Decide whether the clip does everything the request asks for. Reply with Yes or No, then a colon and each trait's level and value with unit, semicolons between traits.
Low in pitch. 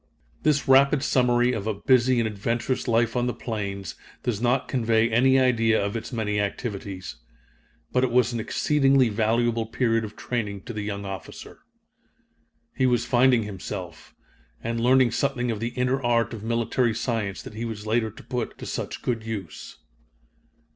Yes: low, 115 Hz